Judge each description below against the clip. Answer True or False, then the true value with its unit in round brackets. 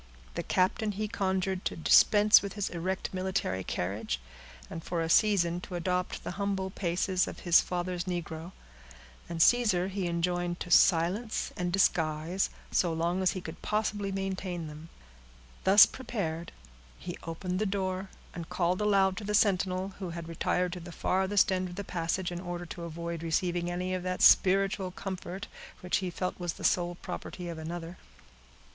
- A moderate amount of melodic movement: False (2.0 semitones)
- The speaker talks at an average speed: True (170 wpm)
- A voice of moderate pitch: True (180 Hz)